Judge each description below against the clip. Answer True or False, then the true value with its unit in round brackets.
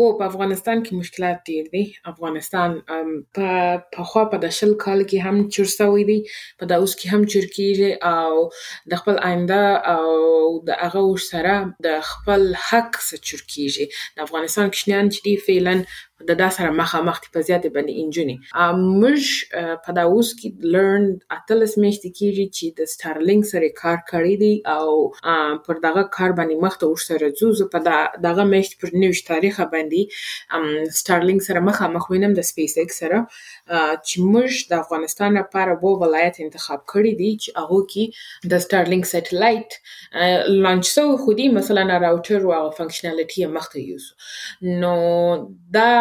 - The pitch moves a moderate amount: True (3.2 semitones)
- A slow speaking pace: False (155 wpm)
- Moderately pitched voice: True (180 Hz)